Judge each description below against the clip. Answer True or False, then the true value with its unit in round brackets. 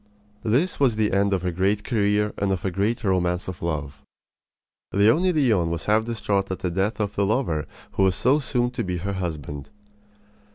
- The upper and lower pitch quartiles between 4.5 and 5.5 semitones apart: False (3.7 semitones)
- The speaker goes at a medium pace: True (195 wpm)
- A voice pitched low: True (100 Hz)